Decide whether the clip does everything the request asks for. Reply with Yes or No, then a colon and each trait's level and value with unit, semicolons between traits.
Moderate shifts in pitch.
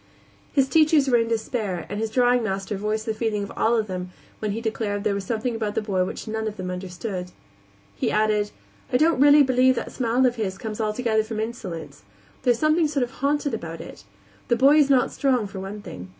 Yes: average, 3.7 semitones